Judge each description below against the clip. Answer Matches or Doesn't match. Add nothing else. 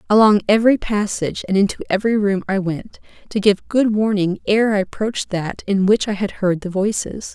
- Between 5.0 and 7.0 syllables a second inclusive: Matches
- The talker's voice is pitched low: Doesn't match